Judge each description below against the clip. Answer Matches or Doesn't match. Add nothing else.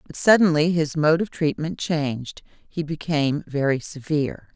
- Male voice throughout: Doesn't match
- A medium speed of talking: Matches